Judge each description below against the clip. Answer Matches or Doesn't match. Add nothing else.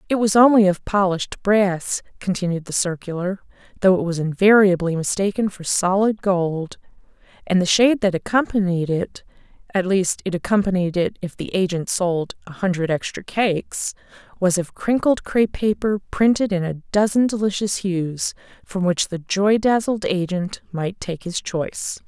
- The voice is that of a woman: Matches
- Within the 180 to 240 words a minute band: Doesn't match